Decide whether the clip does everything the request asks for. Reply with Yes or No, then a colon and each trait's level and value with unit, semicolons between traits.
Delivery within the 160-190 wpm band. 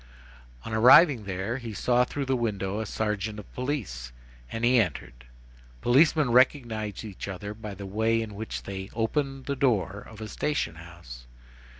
Yes: average, 170 wpm